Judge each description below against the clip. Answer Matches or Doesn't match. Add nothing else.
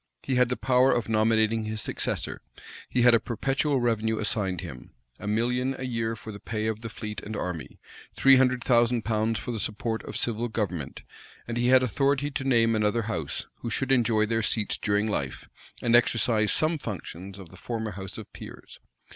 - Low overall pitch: Matches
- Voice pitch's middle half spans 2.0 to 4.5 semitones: Matches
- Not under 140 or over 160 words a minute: Doesn't match